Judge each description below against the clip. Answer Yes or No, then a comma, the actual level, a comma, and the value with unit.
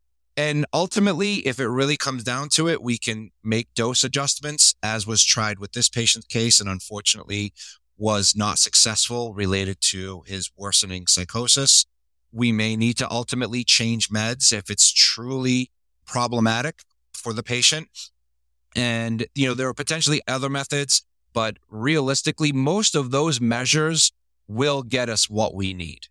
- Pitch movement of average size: Yes, average, 5.0 semitones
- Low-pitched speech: Yes, low, 115 Hz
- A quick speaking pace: No, average, 150 wpm